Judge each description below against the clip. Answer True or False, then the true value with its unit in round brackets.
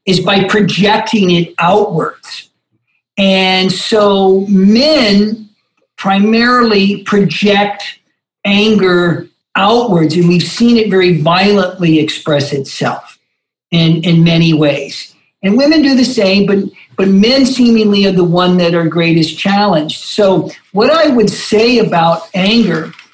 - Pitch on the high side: True (195 Hz)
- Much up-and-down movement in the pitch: False (3.7 semitones)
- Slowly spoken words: True (120 wpm)